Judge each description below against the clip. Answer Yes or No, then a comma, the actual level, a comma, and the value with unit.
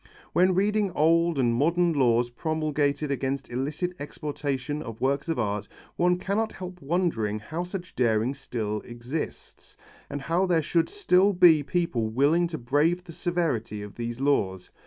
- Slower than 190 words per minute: Yes, average, 155 wpm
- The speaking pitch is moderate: Yes, medium, 150 Hz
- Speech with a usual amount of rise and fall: No, wide, 6.3 semitones